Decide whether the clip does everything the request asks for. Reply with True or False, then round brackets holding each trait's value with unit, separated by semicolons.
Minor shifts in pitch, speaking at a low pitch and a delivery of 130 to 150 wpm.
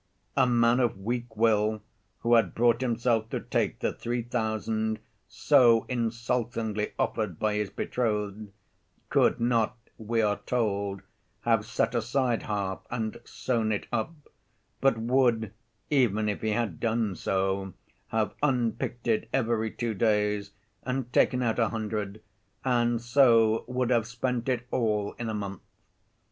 True (2.0 semitones; 115 Hz; 140 wpm)